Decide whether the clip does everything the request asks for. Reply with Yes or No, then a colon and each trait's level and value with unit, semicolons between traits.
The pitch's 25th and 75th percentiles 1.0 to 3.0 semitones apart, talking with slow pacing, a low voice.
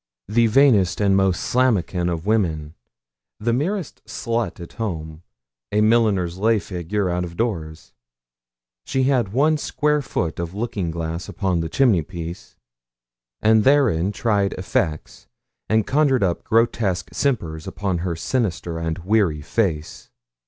No: average, 5.2 semitones; slow, 130 wpm; low, 100 Hz